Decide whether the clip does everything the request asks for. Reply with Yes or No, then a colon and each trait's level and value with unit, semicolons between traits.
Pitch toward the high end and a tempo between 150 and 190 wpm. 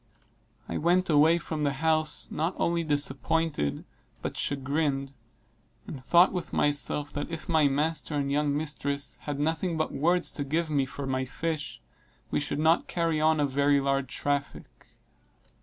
No: medium, 150 Hz; average, 155 wpm